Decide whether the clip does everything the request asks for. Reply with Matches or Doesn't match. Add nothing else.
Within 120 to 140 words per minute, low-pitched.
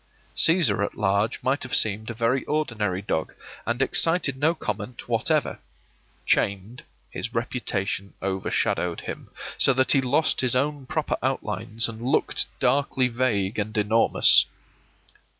Matches